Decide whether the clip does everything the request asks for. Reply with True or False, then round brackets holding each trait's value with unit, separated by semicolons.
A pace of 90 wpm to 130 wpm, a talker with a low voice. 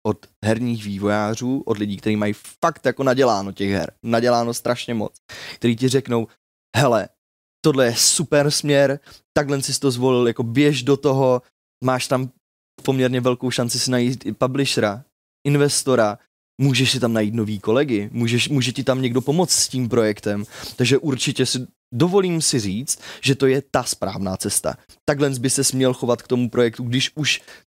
False (170 wpm; 125 Hz)